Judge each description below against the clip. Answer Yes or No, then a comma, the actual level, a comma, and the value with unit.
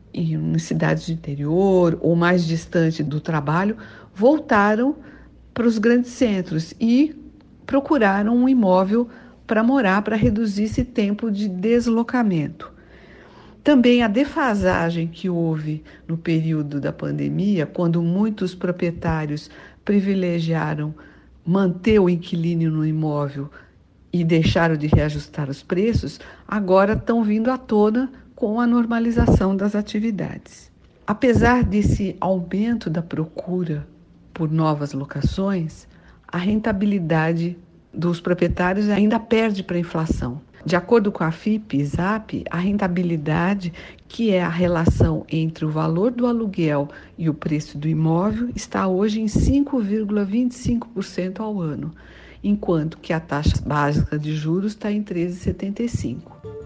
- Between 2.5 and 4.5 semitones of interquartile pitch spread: No, average, 5.3 semitones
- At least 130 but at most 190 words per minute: No, slow, 120 wpm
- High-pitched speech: No, medium, 180 Hz